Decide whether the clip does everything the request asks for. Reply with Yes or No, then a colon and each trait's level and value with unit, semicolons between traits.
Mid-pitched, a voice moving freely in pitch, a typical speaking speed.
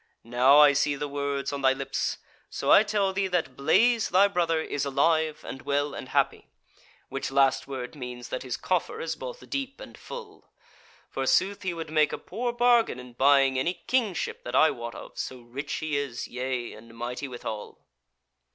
Yes: medium, 145 Hz; wide, 6.2 semitones; average, 185 wpm